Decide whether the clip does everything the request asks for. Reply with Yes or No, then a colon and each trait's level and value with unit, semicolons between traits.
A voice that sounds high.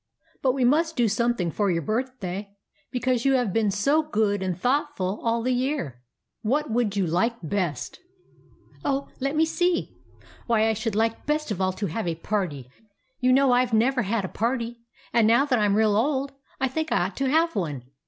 Yes: high, 230 Hz